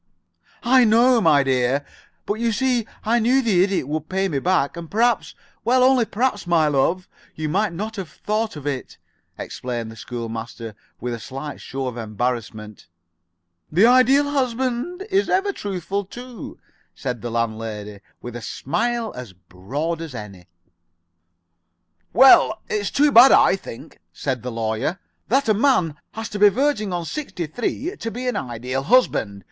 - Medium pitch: Yes, medium, 180 Hz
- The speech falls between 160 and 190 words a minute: Yes, average, 165 wpm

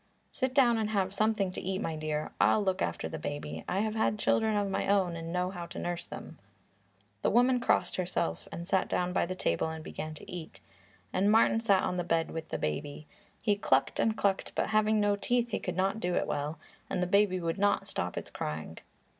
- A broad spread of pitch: No, average, 4.2 semitones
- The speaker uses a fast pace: Yes, fast, 220 wpm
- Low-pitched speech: No, medium, 185 Hz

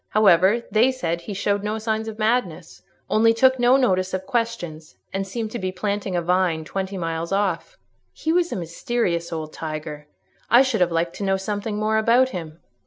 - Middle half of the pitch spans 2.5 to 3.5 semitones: No, average, 4.9 semitones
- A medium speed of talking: Yes, average, 185 wpm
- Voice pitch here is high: Yes, high, 195 Hz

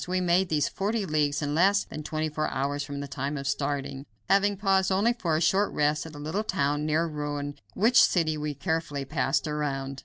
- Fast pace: Yes, fast, 210 wpm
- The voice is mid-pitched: Yes, medium, 155 Hz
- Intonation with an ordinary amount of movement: Yes, average, 4.4 semitones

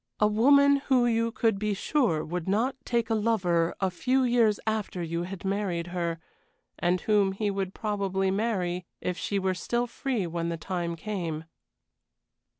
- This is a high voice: Yes, high, 195 Hz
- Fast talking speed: No, average, 165 wpm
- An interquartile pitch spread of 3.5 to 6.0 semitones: Yes, average, 4.4 semitones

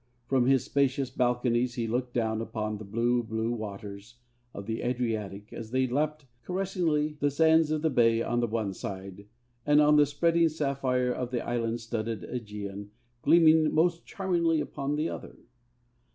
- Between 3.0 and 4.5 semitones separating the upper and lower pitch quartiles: No, average, 5.0 semitones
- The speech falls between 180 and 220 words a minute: No, average, 165 wpm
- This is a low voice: Yes, low, 125 Hz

